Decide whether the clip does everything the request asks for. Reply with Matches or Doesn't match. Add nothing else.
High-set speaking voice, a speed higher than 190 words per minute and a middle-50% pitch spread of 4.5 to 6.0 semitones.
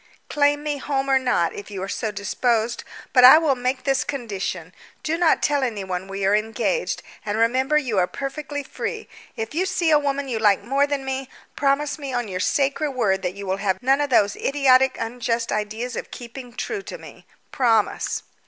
Matches